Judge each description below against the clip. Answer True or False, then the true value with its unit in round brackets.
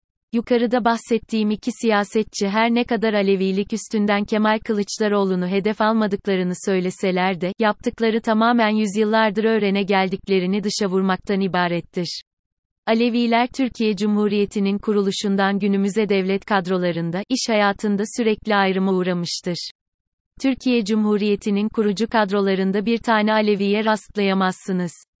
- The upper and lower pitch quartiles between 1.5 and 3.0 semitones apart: True (2.4 semitones)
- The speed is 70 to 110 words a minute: True (100 wpm)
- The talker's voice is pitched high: True (205 Hz)